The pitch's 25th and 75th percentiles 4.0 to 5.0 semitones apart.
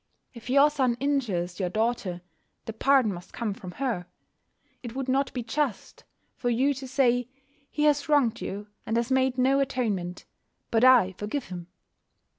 Yes: average, 4.4 semitones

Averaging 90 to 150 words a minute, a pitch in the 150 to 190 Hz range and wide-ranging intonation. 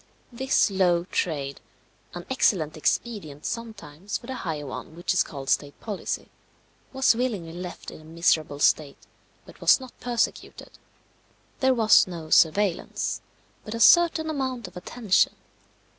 Yes: average, 140 wpm; medium, 185 Hz; wide, 7.1 semitones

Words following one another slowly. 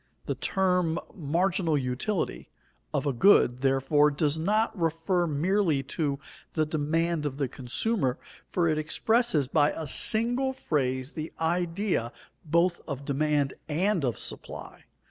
Yes: slow, 130 wpm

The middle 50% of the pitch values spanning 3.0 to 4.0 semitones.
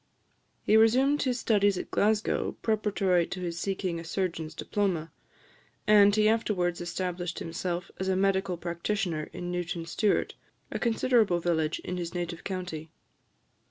Yes: average, 3.3 semitones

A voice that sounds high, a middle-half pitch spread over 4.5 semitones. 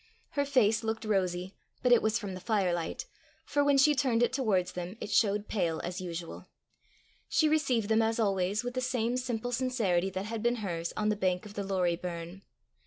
Yes: high, 210 Hz; average, 4.9 semitones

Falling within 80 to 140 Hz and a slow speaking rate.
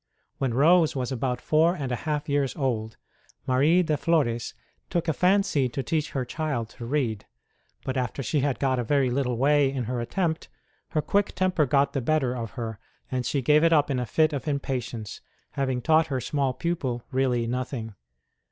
No: low, 135 Hz; average, 190 wpm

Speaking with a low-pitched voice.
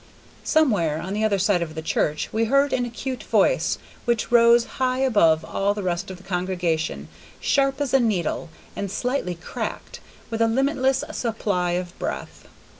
No: high, 215 Hz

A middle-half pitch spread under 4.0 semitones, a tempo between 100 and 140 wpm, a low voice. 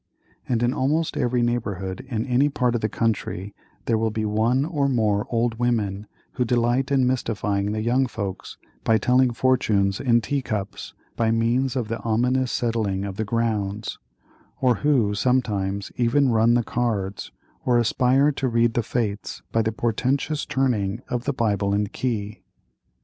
No: average, 3.2 semitones; average, 160 wpm; low, 115 Hz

